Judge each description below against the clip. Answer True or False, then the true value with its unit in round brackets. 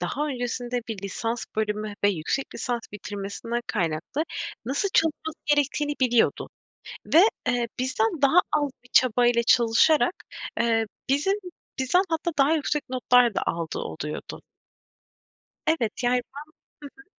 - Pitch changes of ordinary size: True (4.7 semitones)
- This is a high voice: True (250 Hz)